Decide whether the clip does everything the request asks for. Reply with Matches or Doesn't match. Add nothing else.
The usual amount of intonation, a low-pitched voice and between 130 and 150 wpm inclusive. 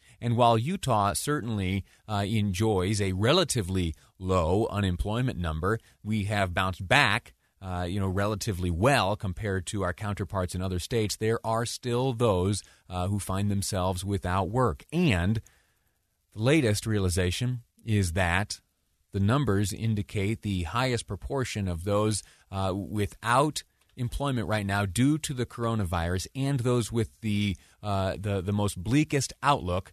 Matches